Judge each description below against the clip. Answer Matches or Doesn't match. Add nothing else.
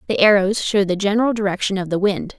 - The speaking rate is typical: Doesn't match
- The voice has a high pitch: Matches